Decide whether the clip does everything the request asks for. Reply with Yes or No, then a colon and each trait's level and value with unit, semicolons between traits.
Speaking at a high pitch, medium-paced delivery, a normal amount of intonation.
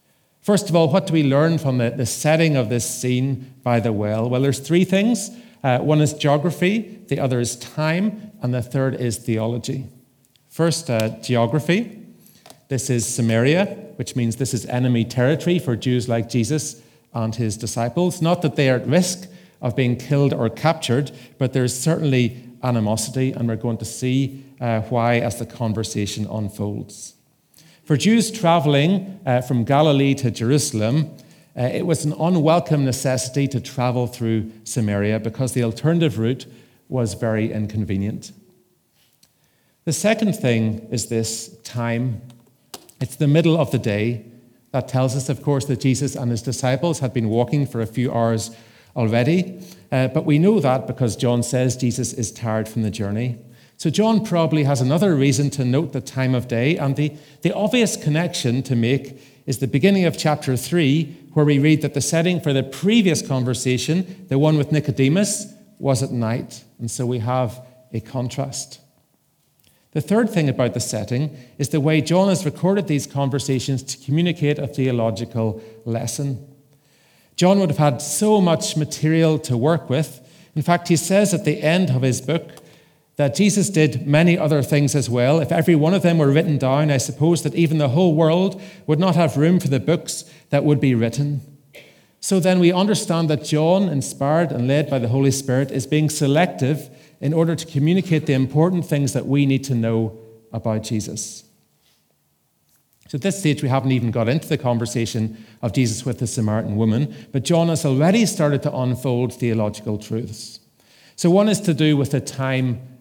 No: low, 135 Hz; average, 175 wpm; average, 4.7 semitones